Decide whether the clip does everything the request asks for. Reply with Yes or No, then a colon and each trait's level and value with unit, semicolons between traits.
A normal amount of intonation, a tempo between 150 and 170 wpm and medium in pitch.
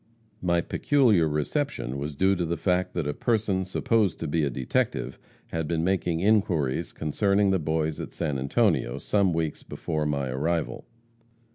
No: average, 4.4 semitones; average, 160 wpm; very low, 85 Hz